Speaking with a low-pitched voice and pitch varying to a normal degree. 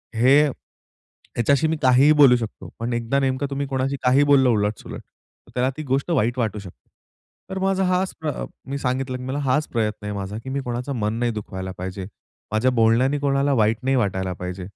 Yes: low, 125 Hz; average, 4.2 semitones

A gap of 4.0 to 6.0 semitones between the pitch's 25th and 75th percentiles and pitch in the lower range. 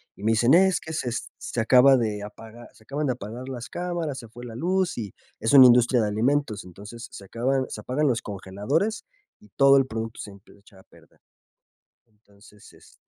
Yes: average, 4.5 semitones; low, 120 Hz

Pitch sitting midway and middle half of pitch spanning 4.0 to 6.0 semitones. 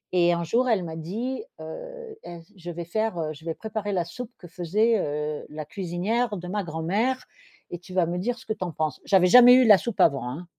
Yes: medium, 180 Hz; average, 5.1 semitones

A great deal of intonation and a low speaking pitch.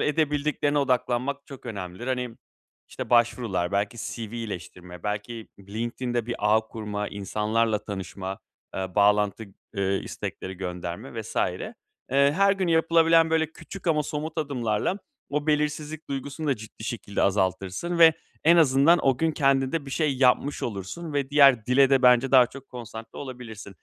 Yes: wide, 5.9 semitones; low, 125 Hz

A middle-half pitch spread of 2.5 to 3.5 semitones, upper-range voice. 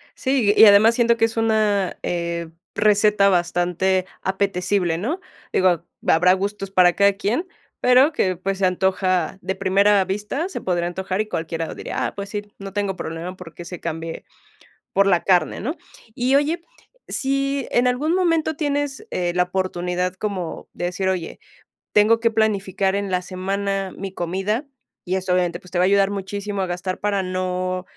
Yes: average, 2.8 semitones; high, 195 Hz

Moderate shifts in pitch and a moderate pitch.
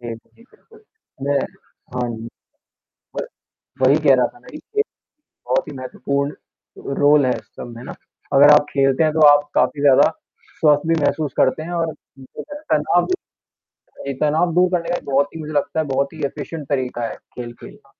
Yes: average, 3.1 semitones; medium, 145 Hz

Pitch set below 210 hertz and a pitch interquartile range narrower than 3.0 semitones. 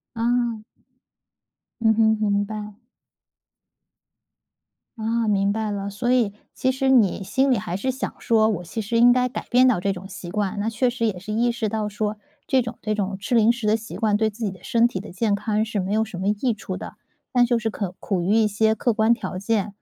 No: high, 220 Hz; narrow, 2.5 semitones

